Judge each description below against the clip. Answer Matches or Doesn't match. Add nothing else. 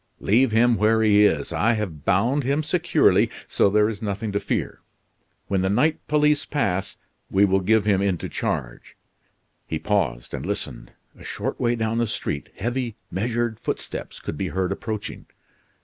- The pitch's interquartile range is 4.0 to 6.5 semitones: Doesn't match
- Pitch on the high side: Doesn't match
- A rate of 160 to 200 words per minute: Matches